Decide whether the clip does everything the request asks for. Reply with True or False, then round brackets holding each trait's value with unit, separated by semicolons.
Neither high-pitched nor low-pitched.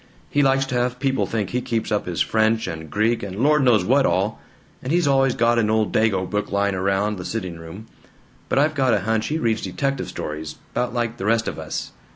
False (110 Hz)